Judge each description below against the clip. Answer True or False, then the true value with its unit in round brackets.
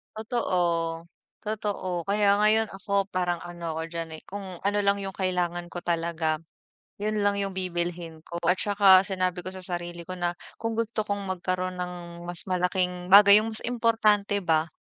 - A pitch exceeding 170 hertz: True (185 Hz)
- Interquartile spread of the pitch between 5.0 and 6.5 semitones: False (2.7 semitones)